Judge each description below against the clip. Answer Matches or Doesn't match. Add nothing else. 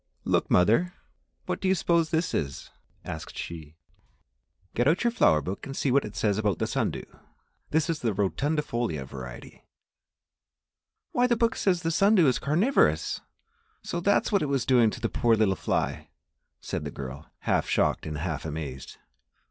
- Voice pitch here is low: Matches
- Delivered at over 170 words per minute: Matches